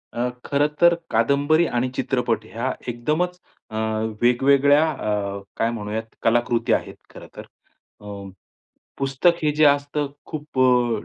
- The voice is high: No, low, 130 Hz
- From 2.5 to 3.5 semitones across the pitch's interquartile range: No, average, 4.0 semitones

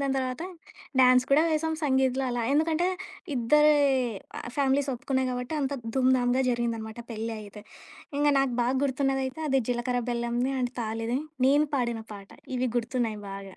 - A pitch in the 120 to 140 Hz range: No, very high, 255 Hz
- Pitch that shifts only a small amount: Yes, narrow, 2.3 semitones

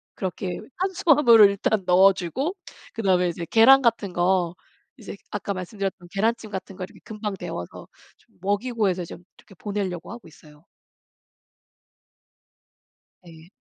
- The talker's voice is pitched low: No, high, 195 Hz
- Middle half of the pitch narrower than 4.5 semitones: Yes, average, 3.9 semitones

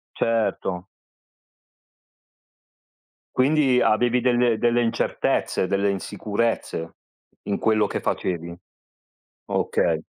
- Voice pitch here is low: Yes, low, 110 Hz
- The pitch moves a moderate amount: Yes, average, 3.7 semitones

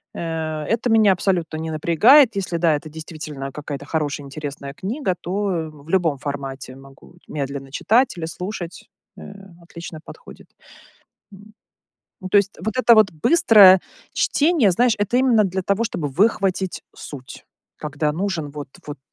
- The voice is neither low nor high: Yes, medium, 170 Hz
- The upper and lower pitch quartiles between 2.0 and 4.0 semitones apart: No, wide, 5.4 semitones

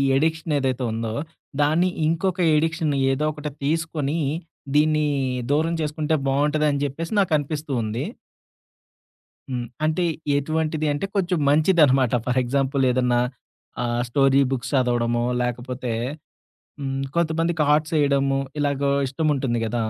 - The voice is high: No, medium, 145 Hz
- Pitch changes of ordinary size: Yes, average, 3.2 semitones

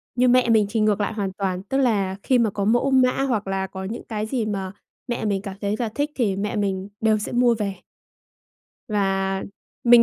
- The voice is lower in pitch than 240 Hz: Yes, high, 210 Hz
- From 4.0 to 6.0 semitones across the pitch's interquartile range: No, average, 3.5 semitones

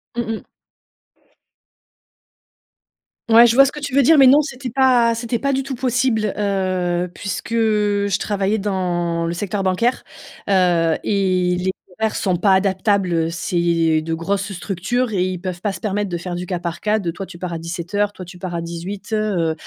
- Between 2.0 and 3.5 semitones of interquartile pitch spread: No, average, 3.9 semitones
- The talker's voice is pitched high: Yes, high, 195 Hz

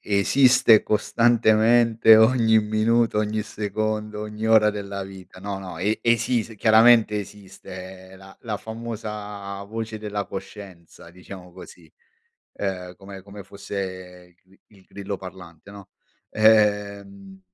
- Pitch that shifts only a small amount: Yes, narrow, 2.2 semitones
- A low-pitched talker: Yes, low, 105 Hz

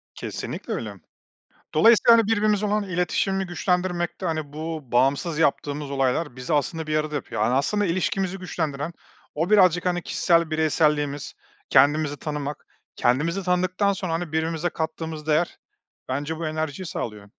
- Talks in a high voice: No, medium, 160 Hz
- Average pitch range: Yes, average, 3.5 semitones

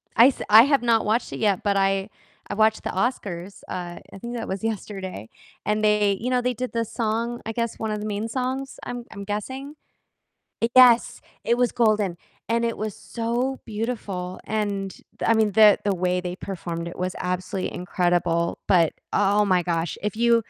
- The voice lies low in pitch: No, high, 210 Hz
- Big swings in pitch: No, average, 3.7 semitones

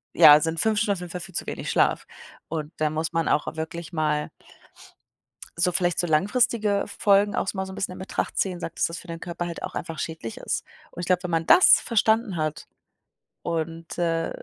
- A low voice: No, medium, 170 Hz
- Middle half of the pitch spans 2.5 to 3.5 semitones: Yes, average, 2.9 semitones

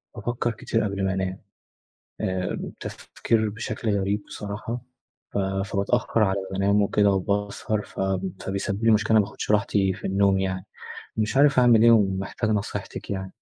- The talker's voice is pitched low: Yes, low, 100 Hz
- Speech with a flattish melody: Yes, narrow, 2.1 semitones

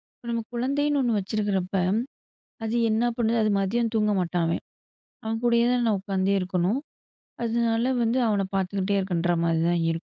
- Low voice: No, high, 210 Hz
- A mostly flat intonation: No, average, 3.8 semitones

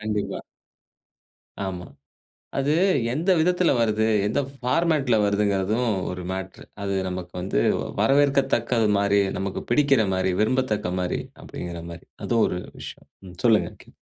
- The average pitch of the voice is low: Yes, low, 110 Hz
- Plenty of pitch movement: Yes, wide, 5.7 semitones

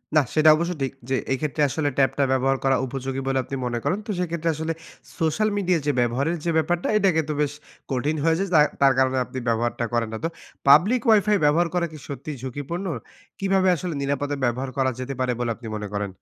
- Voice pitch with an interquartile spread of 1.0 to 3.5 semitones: No, average, 4.4 semitones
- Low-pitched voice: No, medium, 145 Hz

